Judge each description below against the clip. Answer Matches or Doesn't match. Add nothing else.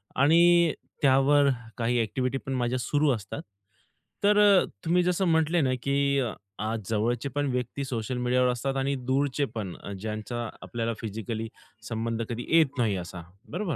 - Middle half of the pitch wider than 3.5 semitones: Matches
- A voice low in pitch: Matches